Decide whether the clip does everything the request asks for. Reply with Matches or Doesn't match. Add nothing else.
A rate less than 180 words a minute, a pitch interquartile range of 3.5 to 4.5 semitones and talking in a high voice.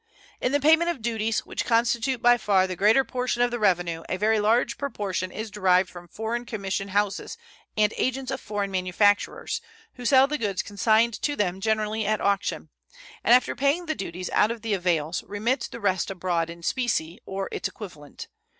Doesn't match